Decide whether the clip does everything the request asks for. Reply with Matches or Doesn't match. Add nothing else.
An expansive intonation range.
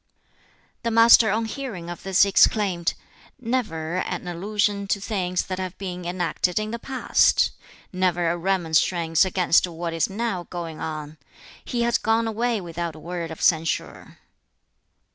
Doesn't match